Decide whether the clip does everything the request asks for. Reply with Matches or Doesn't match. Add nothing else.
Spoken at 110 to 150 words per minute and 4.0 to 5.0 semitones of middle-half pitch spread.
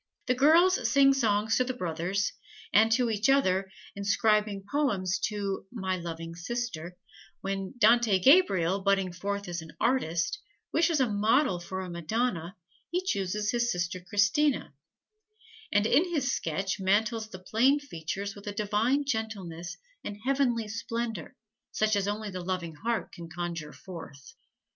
Matches